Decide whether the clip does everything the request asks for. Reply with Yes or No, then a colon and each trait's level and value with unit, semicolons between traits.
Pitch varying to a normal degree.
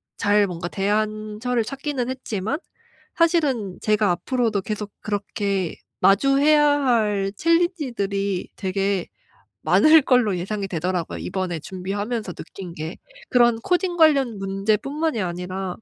Yes: average, 5.0 semitones